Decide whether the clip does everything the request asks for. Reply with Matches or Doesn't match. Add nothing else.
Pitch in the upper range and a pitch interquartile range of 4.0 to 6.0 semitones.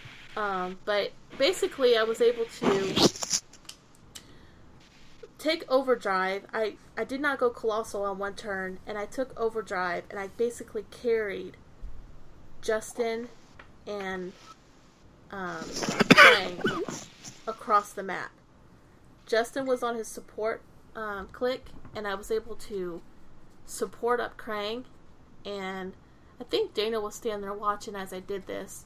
Doesn't match